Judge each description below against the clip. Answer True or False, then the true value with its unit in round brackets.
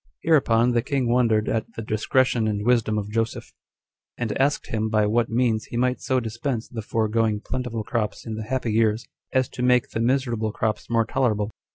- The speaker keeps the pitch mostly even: True (2.3 semitones)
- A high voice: False (115 Hz)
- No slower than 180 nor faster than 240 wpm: True (195 wpm)